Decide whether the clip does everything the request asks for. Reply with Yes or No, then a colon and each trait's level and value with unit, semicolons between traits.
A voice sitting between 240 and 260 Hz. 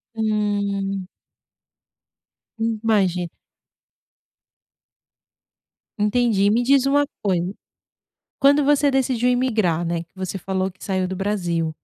No: high, 205 Hz